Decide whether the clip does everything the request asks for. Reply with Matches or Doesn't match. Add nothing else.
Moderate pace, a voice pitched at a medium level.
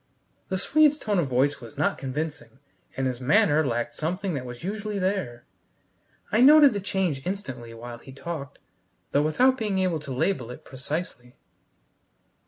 Matches